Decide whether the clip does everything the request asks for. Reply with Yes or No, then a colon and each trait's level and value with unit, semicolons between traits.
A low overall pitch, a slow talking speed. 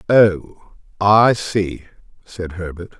Yes: very low, 95 Hz; slow, 100 wpm